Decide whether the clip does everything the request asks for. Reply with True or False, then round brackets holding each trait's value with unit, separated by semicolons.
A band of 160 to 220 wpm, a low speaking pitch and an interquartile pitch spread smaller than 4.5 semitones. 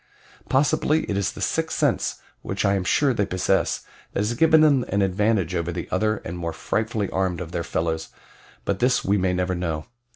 True (200 wpm; 95 Hz; 3.9 semitones)